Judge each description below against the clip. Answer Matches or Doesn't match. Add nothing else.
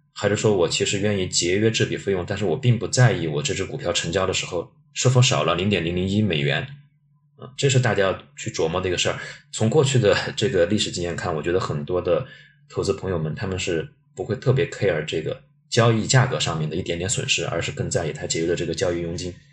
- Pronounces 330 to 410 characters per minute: Matches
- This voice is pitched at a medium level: Doesn't match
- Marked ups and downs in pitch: Matches